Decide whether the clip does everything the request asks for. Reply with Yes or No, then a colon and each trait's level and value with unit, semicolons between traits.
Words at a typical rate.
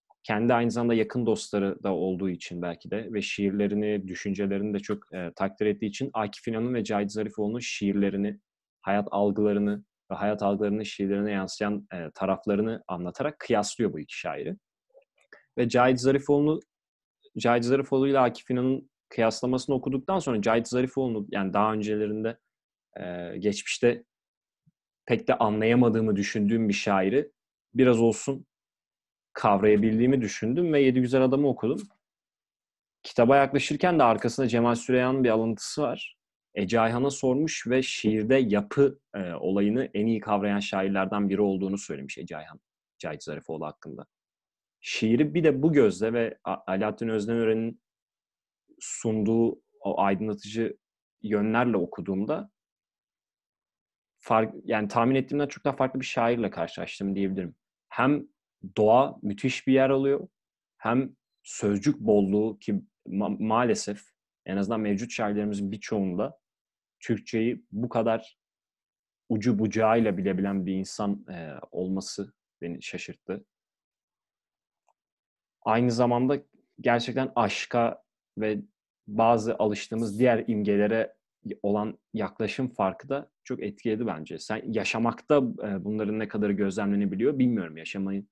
Yes: average, 120 wpm